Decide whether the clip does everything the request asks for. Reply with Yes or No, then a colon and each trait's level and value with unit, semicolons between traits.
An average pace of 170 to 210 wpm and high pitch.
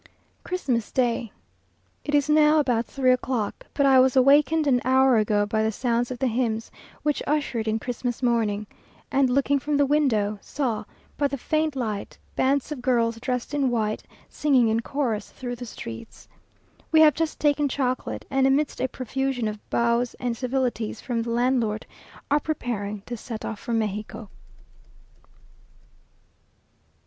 No: average, 155 wpm; very high, 250 Hz